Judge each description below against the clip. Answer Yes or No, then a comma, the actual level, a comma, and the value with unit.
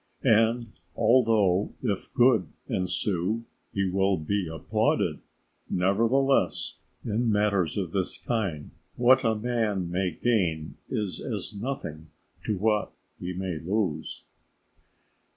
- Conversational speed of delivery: No, slow, 110 wpm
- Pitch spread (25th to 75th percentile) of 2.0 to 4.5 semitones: Yes, average, 3.9 semitones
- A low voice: Yes, low, 100 Hz